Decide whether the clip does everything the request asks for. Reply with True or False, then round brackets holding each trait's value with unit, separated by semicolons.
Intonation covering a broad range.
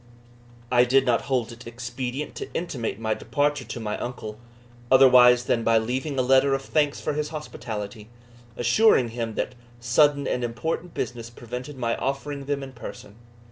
False (3.0 semitones)